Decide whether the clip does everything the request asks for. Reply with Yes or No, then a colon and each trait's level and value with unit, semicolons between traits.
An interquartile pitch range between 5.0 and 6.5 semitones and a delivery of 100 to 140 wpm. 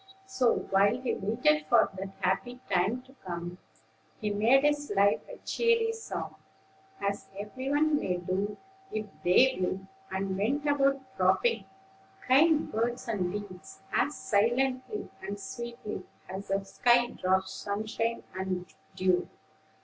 Yes: average, 5.3 semitones; slow, 135 wpm